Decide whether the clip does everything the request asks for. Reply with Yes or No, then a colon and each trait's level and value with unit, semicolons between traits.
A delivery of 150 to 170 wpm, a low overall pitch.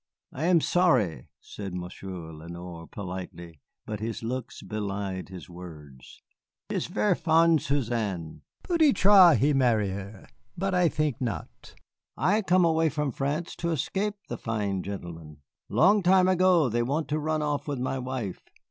Yes: average, 155 wpm; low, 125 Hz